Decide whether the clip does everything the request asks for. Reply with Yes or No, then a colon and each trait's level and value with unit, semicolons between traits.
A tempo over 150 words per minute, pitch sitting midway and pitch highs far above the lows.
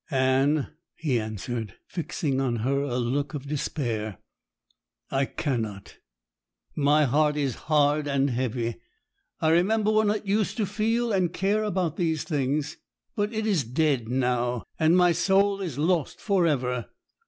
No: average, 145 wpm; medium, 145 Hz; wide, 6.0 semitones